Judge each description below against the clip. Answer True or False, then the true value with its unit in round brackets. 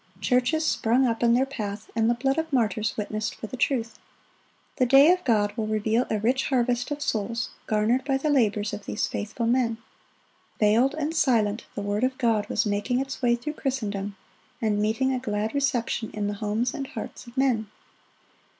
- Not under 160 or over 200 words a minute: True (190 wpm)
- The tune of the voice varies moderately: True (3.6 semitones)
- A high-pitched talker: True (235 Hz)